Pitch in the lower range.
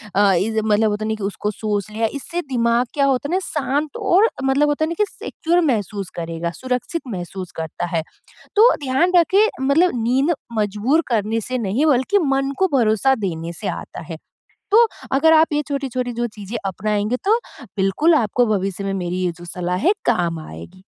No: high, 230 Hz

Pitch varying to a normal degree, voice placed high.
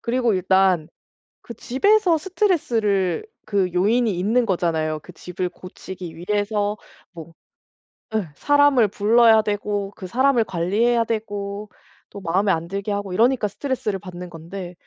Yes: average, 4.3 semitones; high, 205 Hz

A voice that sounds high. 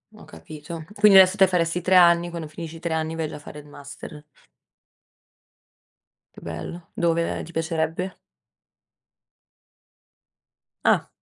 No: medium, 165 Hz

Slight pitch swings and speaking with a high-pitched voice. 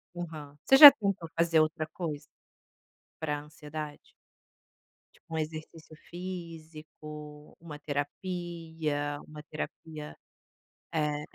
No: narrow, 1.9 semitones; medium, 155 Hz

